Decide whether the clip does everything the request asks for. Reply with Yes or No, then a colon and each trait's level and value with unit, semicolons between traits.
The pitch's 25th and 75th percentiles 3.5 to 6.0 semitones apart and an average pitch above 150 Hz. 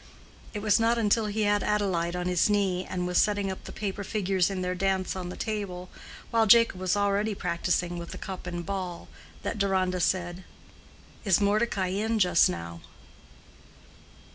No: narrow, 2.5 semitones; high, 190 Hz